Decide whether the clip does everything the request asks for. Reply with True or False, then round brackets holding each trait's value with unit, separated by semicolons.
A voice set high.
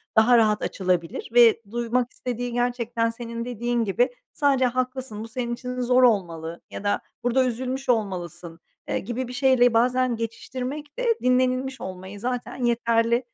True (240 Hz)